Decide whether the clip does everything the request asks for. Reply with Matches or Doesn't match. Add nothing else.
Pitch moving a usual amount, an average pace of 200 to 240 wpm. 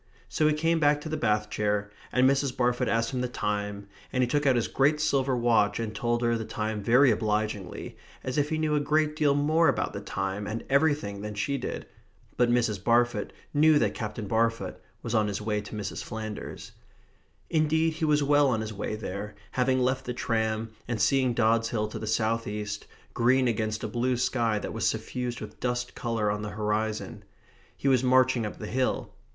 Matches